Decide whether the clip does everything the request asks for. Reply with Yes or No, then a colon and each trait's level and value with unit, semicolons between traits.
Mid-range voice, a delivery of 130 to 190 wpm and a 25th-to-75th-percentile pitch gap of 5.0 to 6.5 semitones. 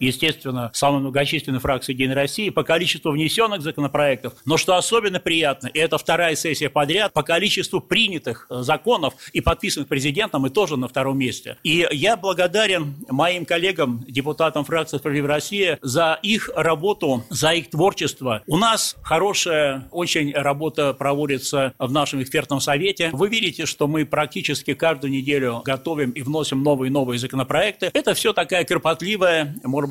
No: medium, 150 Hz; average, 155 wpm; average, 3.5 semitones